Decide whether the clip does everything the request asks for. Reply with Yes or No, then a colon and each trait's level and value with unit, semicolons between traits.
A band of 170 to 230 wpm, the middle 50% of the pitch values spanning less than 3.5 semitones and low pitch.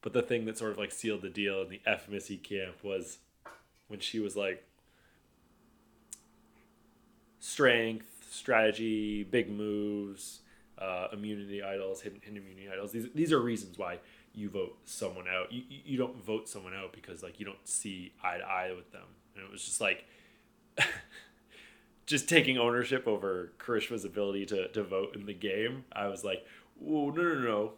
Yes: average, 175 wpm; average, 2.7 semitones; low, 105 Hz